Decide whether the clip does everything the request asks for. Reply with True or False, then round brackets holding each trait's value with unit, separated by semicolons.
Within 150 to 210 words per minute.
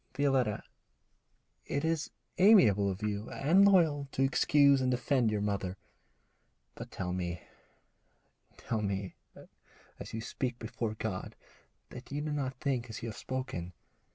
False (140 wpm)